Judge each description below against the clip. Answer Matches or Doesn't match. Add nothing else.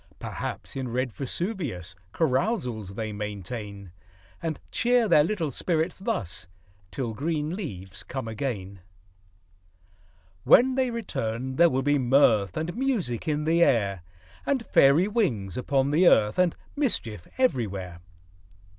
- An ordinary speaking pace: Doesn't match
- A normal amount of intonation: Doesn't match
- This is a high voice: Doesn't match